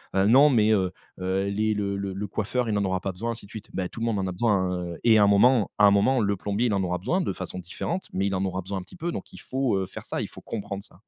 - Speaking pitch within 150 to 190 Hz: No, low, 100 Hz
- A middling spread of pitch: Yes, average, 3.2 semitones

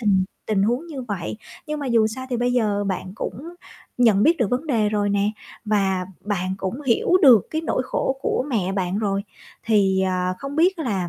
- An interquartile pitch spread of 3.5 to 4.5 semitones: No, average, 4.9 semitones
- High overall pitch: Yes, high, 215 Hz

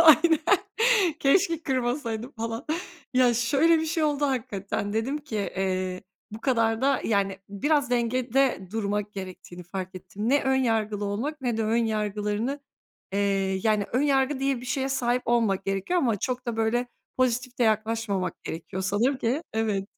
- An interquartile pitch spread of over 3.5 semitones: Yes, average, 4.5 semitones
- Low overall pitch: No, high, 230 Hz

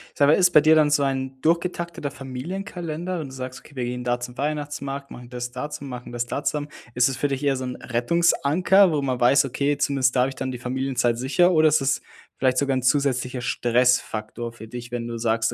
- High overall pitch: No, low, 135 Hz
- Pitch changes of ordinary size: Yes, average, 3.2 semitones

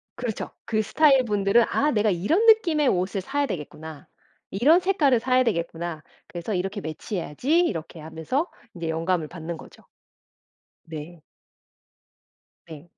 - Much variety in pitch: Yes, wide, 8.0 semitones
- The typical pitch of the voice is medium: No, high, 195 Hz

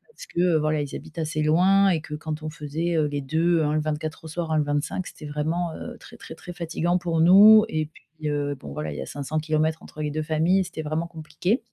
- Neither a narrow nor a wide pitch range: No, narrow, 2.2 semitones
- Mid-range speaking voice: Yes, medium, 155 Hz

